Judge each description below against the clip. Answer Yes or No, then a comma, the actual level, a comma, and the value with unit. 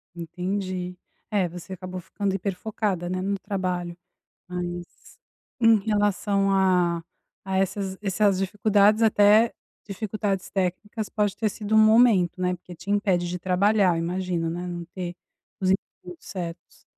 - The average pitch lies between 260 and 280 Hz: No, high, 190 Hz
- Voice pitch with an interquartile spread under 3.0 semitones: Yes, narrow, 2.4 semitones